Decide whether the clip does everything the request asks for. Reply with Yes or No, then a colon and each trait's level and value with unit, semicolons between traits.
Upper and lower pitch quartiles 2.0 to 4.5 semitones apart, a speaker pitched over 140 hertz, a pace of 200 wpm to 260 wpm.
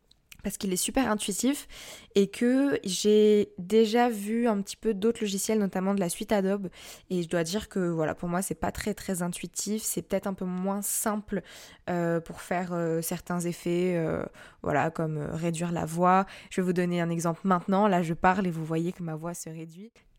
Yes: average, 3.3 semitones; medium, 185 Hz; average, 210 wpm